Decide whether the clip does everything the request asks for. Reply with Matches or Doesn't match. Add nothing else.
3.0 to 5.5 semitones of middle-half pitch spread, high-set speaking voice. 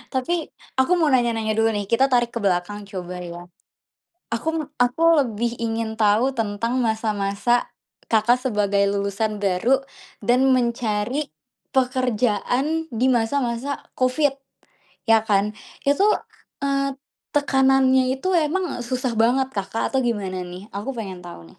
Matches